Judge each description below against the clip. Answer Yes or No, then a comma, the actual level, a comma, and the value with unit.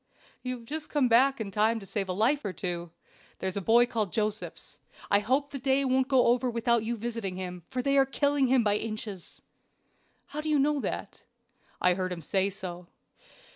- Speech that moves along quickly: Yes, fast, 210 wpm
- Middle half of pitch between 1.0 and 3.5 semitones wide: No, average, 5.1 semitones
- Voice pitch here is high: Yes, high, 230 Hz